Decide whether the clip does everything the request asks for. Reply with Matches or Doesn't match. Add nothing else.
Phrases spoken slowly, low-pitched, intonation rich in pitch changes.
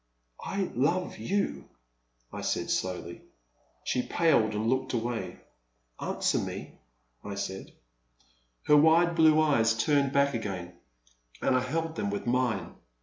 Matches